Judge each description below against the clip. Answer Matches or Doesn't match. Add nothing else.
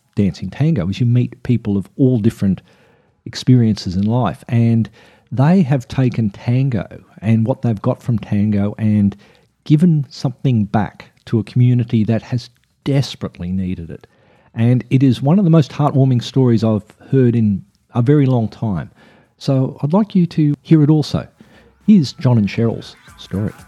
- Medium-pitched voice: Doesn't match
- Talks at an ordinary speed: Matches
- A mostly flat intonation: Doesn't match